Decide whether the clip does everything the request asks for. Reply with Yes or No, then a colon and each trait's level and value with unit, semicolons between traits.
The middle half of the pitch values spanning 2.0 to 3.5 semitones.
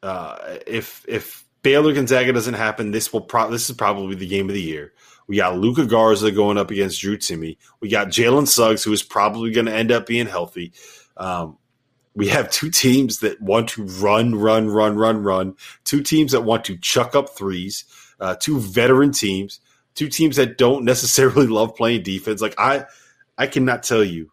No: average, 4.0 semitones